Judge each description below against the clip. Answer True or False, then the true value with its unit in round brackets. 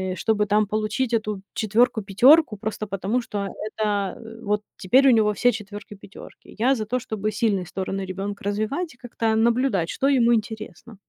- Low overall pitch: False (215 Hz)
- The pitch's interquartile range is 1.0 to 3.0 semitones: True (2.5 semitones)